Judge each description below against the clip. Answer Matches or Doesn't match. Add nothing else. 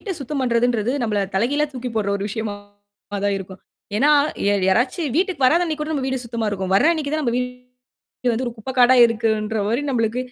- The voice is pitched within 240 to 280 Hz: Matches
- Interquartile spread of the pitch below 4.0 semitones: Matches